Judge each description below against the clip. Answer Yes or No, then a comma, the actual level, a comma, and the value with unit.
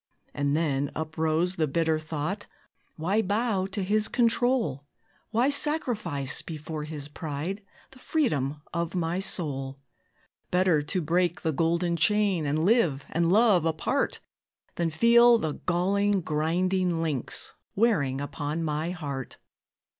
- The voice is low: No, medium, 170 Hz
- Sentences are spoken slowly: Yes, slow, 125 wpm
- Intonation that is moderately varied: Yes, average, 4.7 semitones